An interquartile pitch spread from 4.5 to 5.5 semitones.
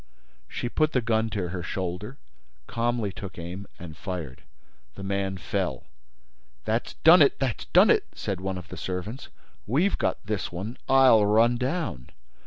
Yes: average, 4.8 semitones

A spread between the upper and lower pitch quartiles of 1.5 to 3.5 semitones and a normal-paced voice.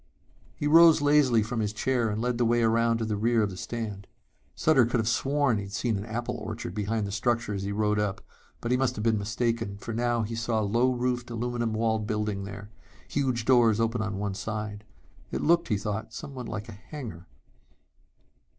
No: narrow, 2.5 semitones; fast, 210 wpm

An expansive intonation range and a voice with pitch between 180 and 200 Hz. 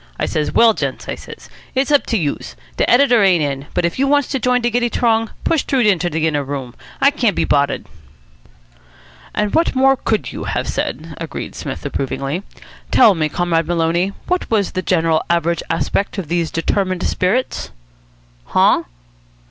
Yes: wide, 6.8 semitones; medium, 185 Hz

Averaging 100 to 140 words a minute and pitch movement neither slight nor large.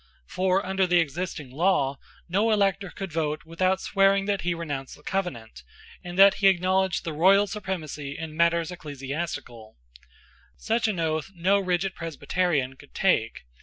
No: average, 150 wpm; average, 3.8 semitones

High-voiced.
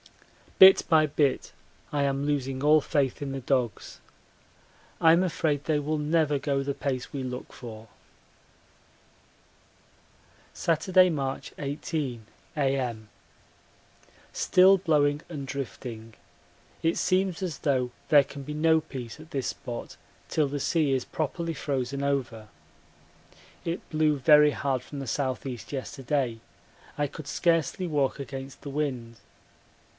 No: medium, 140 Hz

